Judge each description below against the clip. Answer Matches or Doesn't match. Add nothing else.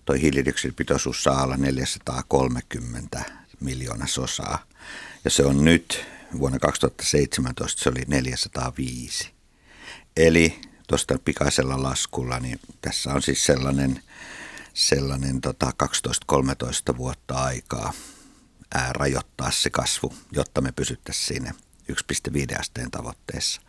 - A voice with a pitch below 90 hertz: Matches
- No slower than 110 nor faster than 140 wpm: Doesn't match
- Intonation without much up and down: Matches